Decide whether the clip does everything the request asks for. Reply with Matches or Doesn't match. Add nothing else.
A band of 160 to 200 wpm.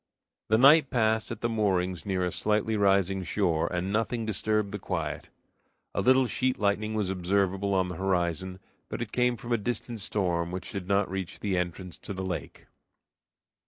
Matches